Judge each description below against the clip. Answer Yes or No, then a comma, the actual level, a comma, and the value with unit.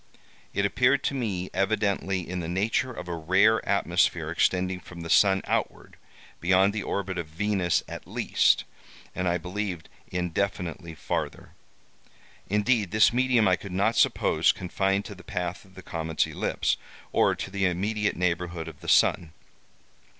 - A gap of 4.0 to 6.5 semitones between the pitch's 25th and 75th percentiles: No, average, 2.7 semitones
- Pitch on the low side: Yes, very low, 95 Hz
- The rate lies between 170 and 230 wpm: No, average, 155 wpm